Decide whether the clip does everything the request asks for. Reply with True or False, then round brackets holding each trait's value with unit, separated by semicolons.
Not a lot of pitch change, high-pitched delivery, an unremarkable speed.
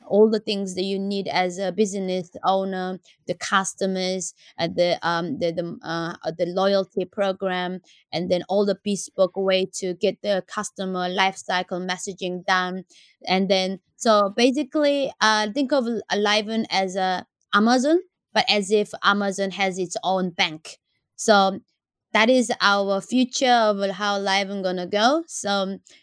True (2.2 semitones; 195 Hz; 150 wpm)